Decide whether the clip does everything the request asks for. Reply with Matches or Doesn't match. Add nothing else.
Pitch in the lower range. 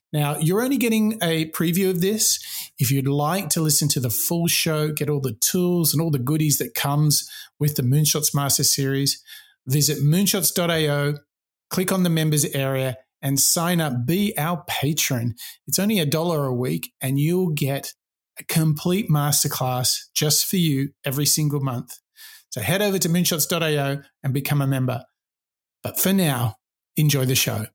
Doesn't match